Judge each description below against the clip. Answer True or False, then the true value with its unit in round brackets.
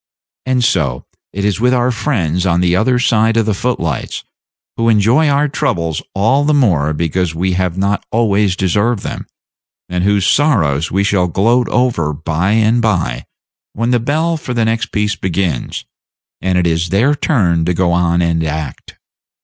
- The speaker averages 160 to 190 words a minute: True (175 wpm)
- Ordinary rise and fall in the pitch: False (5.8 semitones)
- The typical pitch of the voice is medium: False (100 Hz)